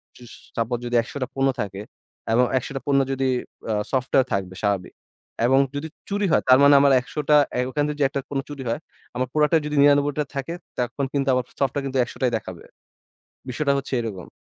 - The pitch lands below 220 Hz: Yes, low, 135 Hz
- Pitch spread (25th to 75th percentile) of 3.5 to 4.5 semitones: No, average, 2.9 semitones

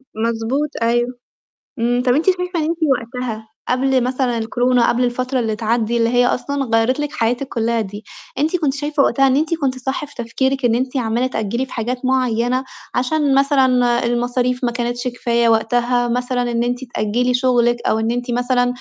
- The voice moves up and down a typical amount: No, narrow, 1.9 semitones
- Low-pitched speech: No, high, 245 Hz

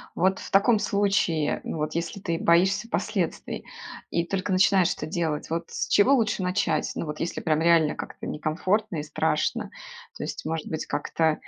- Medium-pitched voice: Yes, medium, 170 Hz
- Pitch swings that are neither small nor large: Yes, average, 3.7 semitones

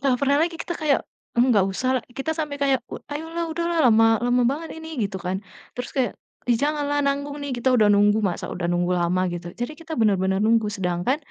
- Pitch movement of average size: No, wide, 6.6 semitones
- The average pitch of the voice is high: Yes, high, 245 Hz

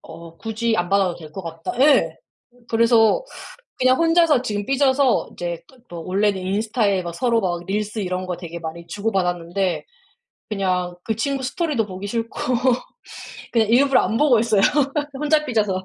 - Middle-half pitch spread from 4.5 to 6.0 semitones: Yes, average, 5.2 semitones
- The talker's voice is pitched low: No, high, 210 Hz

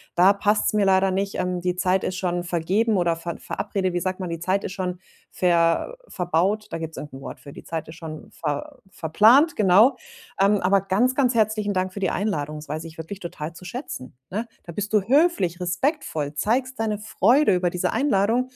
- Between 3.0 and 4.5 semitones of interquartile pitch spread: Yes, average, 3.8 semitones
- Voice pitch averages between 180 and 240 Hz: Yes, medium, 185 Hz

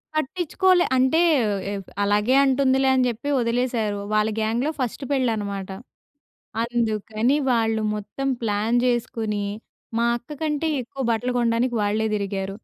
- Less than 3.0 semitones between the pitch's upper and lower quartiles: No, average, 3.6 semitones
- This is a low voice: No, high, 235 Hz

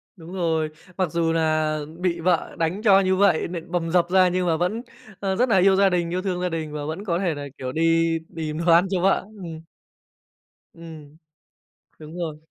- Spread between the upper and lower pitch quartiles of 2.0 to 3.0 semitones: Yes, narrow, 2.6 semitones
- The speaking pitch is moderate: Yes, medium, 170 Hz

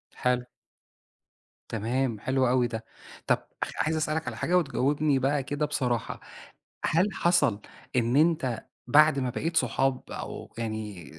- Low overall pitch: Yes, low, 130 Hz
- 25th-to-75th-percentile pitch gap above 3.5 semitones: Yes, average, 4.0 semitones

